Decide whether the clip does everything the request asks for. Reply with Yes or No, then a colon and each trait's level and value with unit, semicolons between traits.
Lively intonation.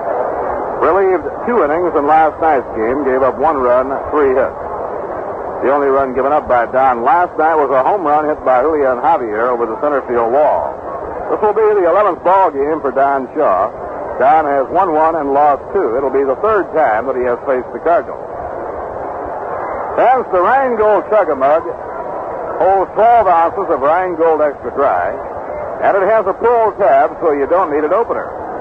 Yes: wide, 7.7 semitones